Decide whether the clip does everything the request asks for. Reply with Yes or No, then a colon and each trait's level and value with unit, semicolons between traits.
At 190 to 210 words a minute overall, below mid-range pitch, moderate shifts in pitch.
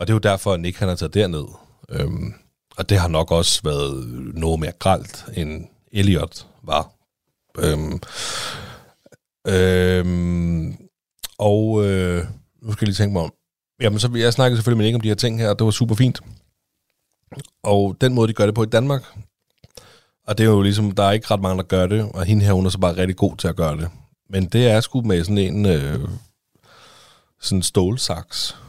Yes: average, 195 wpm; low, 100 Hz; average, 3.6 semitones